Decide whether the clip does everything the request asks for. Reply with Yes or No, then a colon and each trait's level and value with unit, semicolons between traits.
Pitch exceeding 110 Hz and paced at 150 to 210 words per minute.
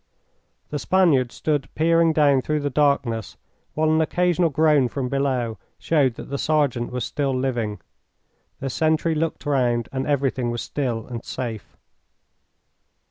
No: medium, 140 Hz; average, 140 wpm